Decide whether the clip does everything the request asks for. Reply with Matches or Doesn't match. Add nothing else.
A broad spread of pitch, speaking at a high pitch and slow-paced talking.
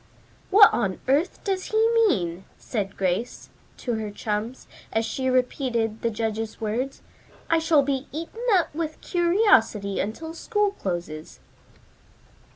Matches